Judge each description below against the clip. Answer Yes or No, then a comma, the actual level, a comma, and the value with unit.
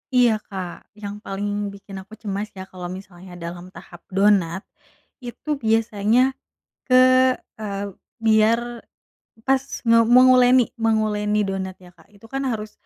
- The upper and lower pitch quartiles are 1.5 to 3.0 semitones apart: Yes, average, 2.7 semitones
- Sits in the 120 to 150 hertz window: No, high, 210 Hz